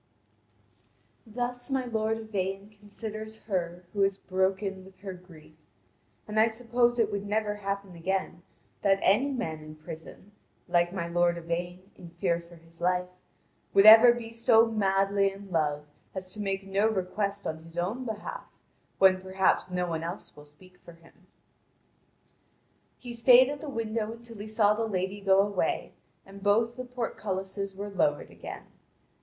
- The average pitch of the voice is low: No, high, 195 Hz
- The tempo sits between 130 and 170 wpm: Yes, average, 160 wpm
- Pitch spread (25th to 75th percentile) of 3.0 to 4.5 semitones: Yes, average, 3.3 semitones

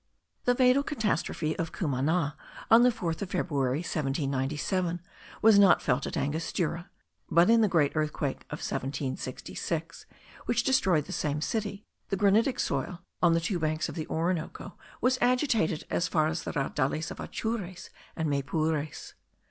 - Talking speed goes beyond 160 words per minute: No, average, 150 wpm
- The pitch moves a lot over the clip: No, average, 5.0 semitones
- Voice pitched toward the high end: No, medium, 165 Hz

